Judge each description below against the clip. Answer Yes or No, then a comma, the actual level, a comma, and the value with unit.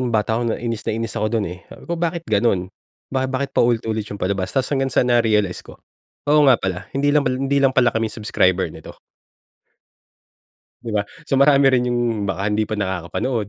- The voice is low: Yes, low, 115 Hz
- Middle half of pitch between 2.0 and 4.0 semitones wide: No, average, 4.4 semitones